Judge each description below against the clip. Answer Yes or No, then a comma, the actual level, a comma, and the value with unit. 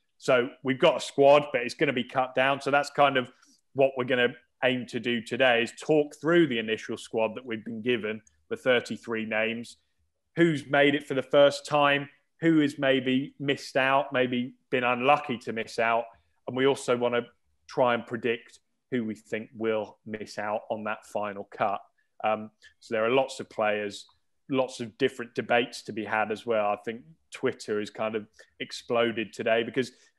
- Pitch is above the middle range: No, low, 125 Hz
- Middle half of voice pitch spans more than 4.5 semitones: No, average, 3.8 semitones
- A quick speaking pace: No, average, 195 wpm